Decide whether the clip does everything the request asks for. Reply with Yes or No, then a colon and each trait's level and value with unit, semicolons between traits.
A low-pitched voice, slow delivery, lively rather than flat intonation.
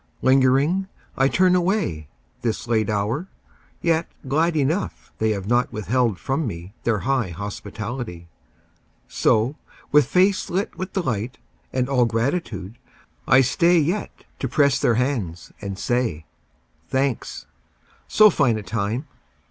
Yes: low, 125 Hz; slow, 130 wpm; wide, 5.9 semitones